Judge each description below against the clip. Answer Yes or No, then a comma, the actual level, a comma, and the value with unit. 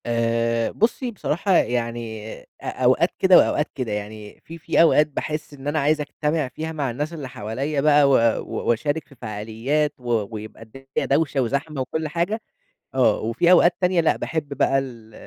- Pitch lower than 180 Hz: Yes, medium, 140 Hz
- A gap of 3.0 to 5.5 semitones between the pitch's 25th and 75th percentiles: Yes, average, 4.9 semitones